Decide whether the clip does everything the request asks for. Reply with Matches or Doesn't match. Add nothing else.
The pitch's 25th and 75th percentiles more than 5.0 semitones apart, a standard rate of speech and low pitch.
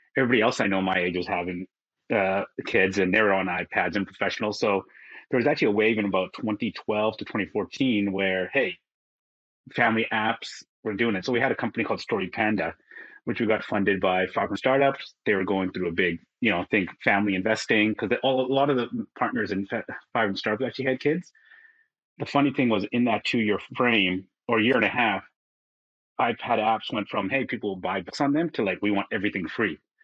Doesn't match